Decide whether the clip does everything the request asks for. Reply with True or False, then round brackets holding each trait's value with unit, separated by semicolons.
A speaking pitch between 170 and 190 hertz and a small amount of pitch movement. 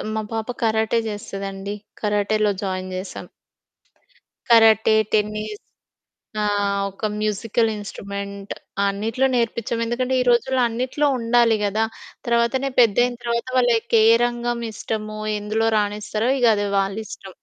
False (220 Hz; 2.3 semitones)